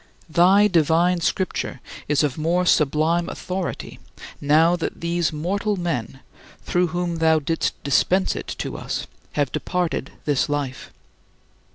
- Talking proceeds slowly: Yes, slow, 130 wpm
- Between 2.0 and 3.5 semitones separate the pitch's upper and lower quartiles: Yes, average, 2.9 semitones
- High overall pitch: No, medium, 165 Hz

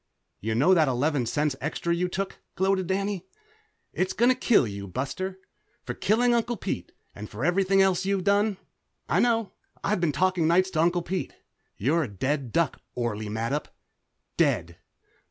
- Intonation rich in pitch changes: Yes, wide, 6.3 semitones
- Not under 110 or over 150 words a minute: No, average, 160 wpm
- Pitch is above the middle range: No, medium, 175 Hz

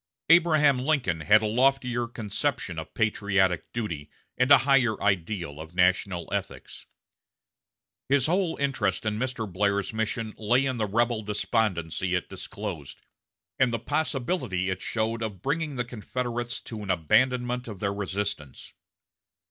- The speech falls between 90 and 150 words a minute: Yes, average, 140 wpm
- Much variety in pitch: No, average, 4.8 semitones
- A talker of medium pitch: No, low, 110 Hz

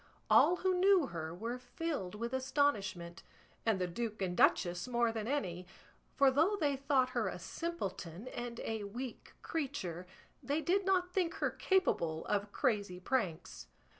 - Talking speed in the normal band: Yes, average, 155 wpm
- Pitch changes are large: Yes, wide, 7.9 semitones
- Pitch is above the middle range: Yes, high, 240 Hz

